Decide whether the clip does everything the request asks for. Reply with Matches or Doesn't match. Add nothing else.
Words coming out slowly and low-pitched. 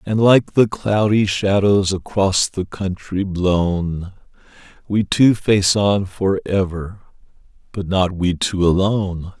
Matches